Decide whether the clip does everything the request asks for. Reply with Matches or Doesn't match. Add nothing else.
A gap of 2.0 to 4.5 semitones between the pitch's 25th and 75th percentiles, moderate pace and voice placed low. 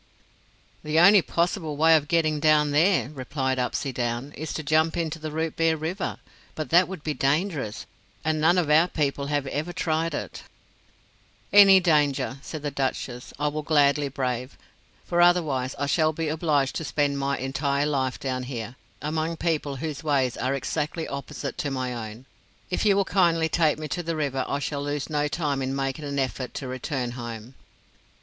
Doesn't match